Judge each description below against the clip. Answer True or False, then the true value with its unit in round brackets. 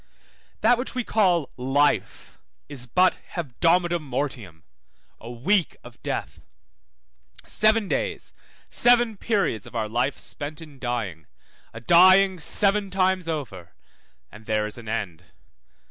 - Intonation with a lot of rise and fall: True (8.2 semitones)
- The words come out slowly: True (125 wpm)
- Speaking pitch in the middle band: True (150 Hz)